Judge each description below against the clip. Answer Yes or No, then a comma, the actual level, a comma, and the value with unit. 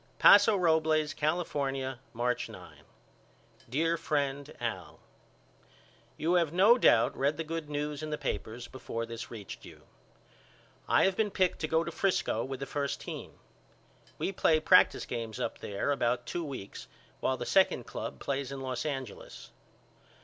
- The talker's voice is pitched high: No, medium, 145 Hz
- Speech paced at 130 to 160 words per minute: Yes, average, 155 wpm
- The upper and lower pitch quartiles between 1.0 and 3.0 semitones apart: No, average, 4.0 semitones